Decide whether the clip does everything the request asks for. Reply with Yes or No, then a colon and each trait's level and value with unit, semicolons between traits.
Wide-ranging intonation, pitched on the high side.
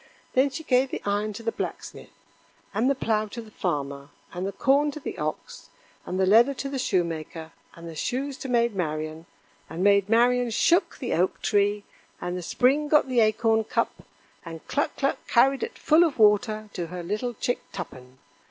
Yes: wide, 6.2 semitones; high, 215 Hz